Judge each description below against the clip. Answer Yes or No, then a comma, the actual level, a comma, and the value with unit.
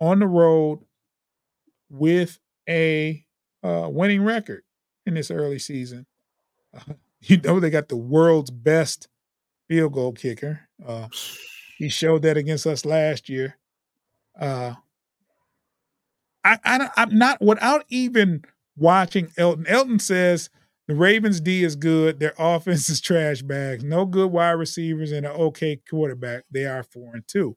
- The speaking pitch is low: No, medium, 160 Hz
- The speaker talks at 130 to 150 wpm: Yes, average, 140 wpm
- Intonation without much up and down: No, average, 3.7 semitones